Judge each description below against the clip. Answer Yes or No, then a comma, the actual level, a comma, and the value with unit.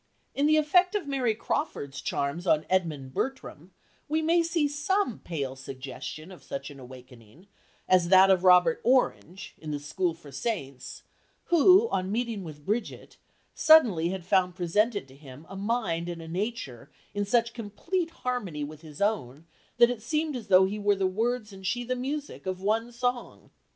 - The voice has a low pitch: No, high, 195 Hz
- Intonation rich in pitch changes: Yes, wide, 7.4 semitones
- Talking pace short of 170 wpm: No, average, 175 wpm